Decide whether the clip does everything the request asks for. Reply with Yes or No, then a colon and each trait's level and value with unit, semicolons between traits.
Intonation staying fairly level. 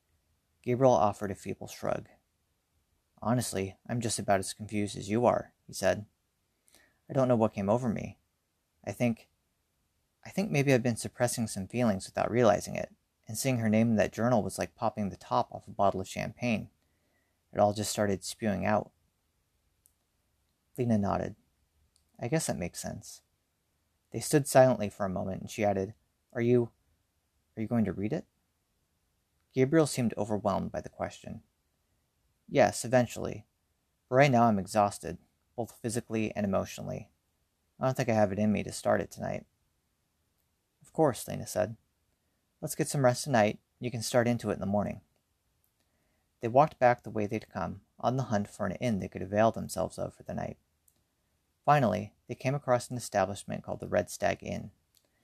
No: average, 5.2 semitones